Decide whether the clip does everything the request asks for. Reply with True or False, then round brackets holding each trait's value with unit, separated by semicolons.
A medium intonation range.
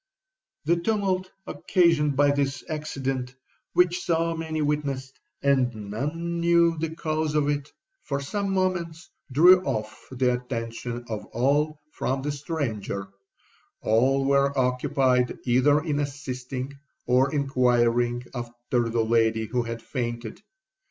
True (4.3 semitones)